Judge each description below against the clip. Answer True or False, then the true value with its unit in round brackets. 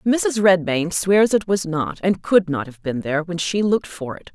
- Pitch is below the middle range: False (175 Hz)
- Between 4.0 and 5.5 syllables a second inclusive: True (4.7 syllables/s)